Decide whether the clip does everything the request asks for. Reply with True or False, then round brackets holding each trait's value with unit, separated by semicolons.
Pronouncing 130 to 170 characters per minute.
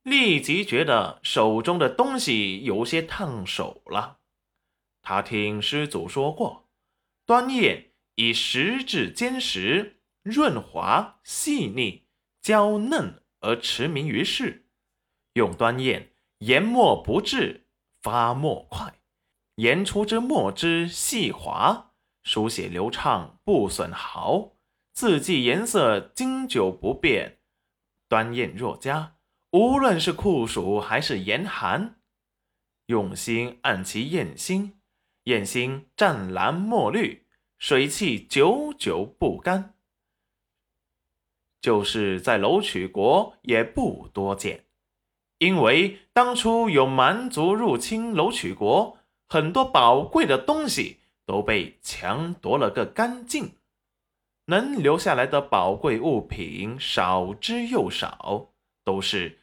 True (155 characters per minute)